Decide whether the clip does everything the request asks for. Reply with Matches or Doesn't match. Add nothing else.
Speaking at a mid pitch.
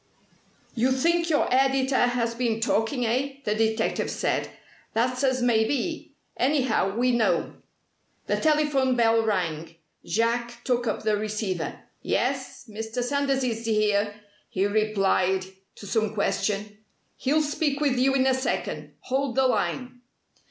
Doesn't match